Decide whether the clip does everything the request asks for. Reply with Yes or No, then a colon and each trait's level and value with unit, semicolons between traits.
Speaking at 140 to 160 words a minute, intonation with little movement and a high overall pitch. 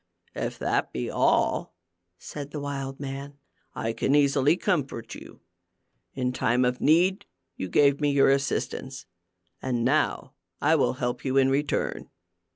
No: average, 145 wpm; narrow, 2.1 semitones; low, 135 Hz